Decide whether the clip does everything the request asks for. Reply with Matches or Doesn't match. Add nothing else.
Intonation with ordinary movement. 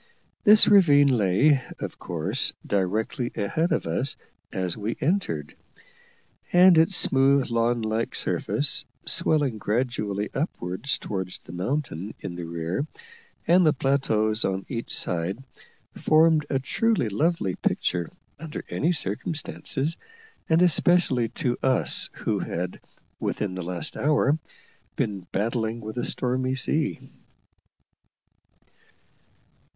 Doesn't match